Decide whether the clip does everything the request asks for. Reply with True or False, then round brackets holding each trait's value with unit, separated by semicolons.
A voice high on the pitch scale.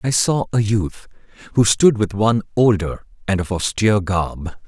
False (105 Hz)